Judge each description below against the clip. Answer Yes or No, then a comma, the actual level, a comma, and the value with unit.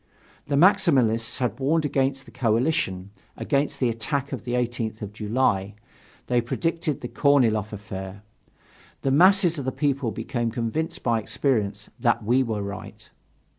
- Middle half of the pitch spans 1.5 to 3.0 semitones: No, average, 4.3 semitones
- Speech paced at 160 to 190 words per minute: No, average, 145 wpm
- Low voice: Yes, low, 120 Hz